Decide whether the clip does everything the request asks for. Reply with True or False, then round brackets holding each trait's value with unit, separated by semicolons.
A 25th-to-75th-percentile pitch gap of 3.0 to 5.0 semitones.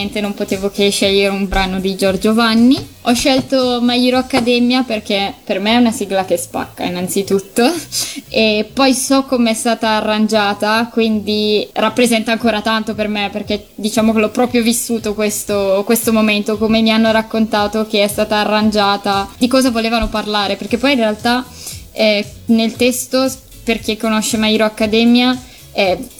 False (2.4 semitones)